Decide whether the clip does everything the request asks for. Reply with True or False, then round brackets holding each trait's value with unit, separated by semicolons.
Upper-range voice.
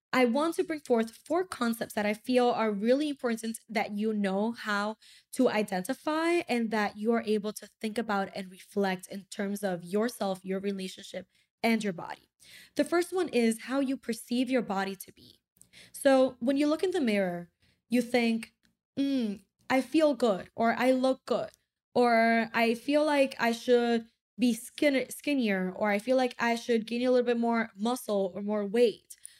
True (230 Hz)